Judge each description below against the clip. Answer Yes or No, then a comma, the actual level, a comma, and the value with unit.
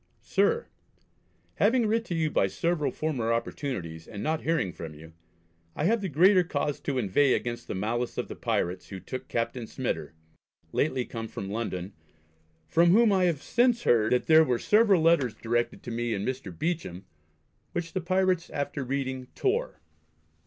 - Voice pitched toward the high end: No, low, 135 Hz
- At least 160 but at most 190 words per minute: Yes, average, 170 wpm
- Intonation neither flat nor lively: No, wide, 7.2 semitones